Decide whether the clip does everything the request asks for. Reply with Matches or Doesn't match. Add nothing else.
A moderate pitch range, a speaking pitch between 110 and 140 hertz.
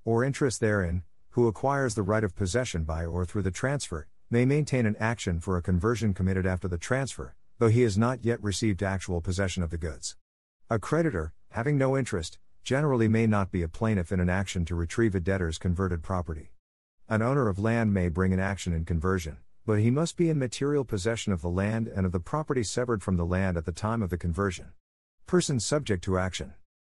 Doesn't match